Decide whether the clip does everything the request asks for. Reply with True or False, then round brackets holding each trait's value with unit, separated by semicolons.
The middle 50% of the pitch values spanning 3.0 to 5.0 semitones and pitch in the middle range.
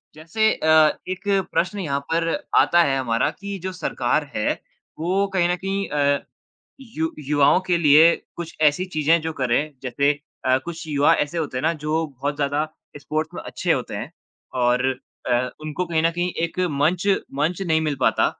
True (3.3 semitones; 155 Hz)